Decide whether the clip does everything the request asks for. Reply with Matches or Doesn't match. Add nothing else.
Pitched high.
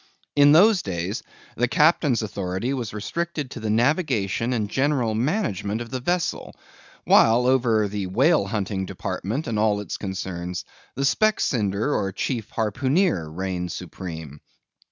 Doesn't match